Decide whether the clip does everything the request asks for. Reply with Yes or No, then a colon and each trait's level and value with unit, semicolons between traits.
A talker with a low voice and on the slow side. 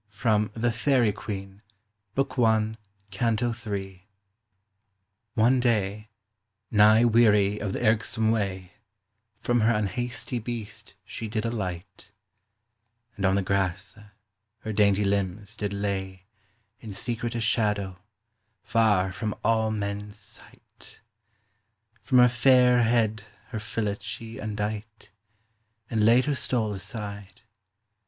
Yes: low, 110 Hz; slow, 115 wpm